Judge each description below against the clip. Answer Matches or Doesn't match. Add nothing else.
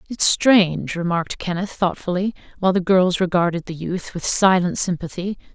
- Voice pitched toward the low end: Doesn't match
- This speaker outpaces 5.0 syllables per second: Matches